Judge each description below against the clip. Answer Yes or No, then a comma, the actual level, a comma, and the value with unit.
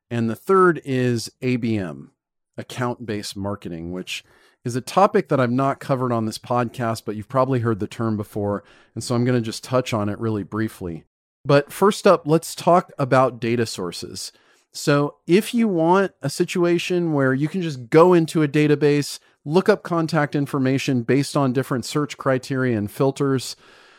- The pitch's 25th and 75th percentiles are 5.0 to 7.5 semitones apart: Yes, wide, 5.5 semitones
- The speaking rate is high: No, average, 175 wpm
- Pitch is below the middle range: Yes, low, 130 Hz